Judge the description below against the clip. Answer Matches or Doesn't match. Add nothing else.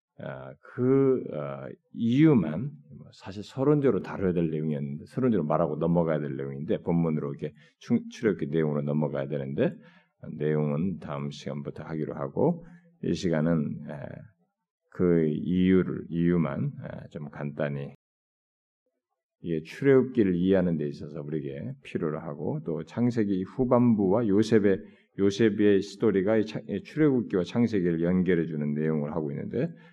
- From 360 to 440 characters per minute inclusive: Doesn't match